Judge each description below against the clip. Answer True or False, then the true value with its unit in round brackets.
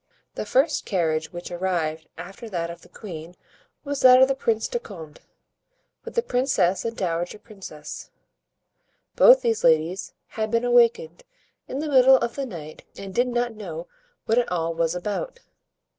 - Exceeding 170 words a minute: False (165 wpm)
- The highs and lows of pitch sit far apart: True (6.4 semitones)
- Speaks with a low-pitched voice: False (205 Hz)